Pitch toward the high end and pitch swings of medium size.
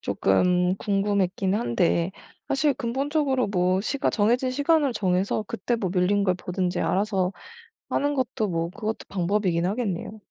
Yes: high, 200 Hz; average, 4.8 semitones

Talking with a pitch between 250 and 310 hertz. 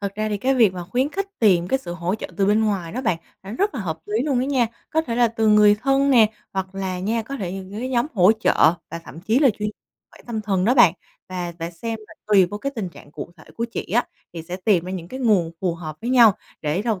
No: high, 210 Hz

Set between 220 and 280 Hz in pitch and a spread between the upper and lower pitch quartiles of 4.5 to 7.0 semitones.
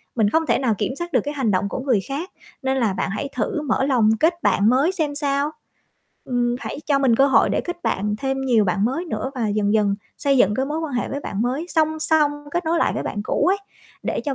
Yes: very high, 270 Hz; average, 5.3 semitones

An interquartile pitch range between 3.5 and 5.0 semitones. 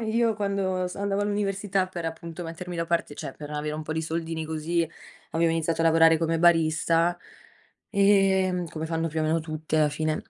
No: average, 2.8 semitones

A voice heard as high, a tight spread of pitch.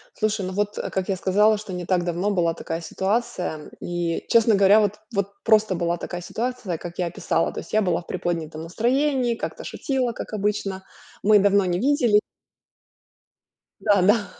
No: high, 200 Hz; average, 3.6 semitones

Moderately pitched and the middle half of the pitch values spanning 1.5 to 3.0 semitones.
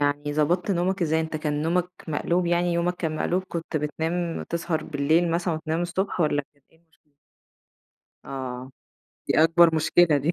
Yes: medium, 165 Hz; narrow, 2.5 semitones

